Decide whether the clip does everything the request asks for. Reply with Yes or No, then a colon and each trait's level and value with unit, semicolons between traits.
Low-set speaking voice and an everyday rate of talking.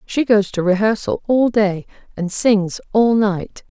No: high, 205 Hz; average, 160 wpm